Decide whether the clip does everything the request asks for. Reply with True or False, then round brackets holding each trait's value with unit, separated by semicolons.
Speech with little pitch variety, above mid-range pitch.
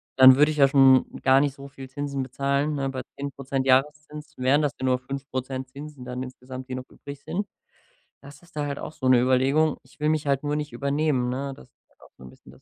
False (2.0 semitones; 135 Hz)